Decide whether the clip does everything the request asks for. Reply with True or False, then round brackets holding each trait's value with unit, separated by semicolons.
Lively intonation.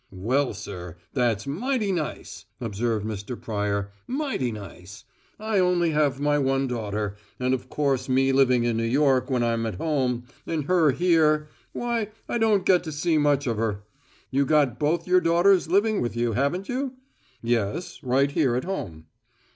True (6.4 semitones)